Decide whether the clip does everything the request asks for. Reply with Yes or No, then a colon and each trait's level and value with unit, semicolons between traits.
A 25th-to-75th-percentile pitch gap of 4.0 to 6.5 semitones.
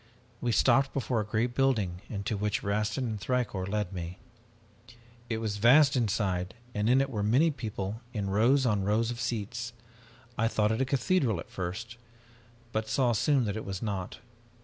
No: average, 3.3 semitones